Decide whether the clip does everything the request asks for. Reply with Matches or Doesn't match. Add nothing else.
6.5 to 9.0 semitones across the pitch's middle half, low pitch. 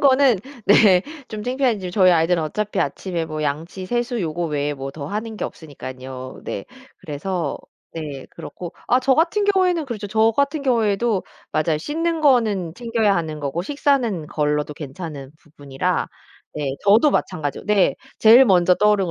Doesn't match